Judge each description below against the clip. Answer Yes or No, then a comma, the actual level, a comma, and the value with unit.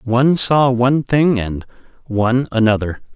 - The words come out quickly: No, slow, 135 wpm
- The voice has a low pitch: Yes, low, 120 Hz